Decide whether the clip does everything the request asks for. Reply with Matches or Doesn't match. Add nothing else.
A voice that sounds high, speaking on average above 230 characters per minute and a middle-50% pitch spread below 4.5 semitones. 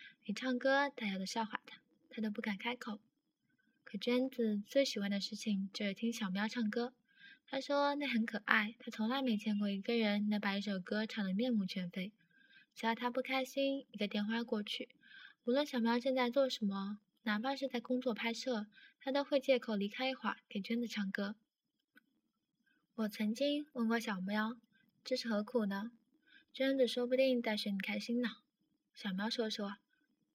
Matches